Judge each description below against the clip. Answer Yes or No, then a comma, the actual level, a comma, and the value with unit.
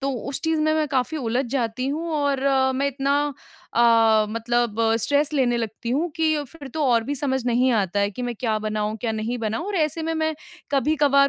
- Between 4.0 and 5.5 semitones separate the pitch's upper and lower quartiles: Yes, average, 4.3 semitones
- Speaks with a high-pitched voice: Yes, very high, 260 Hz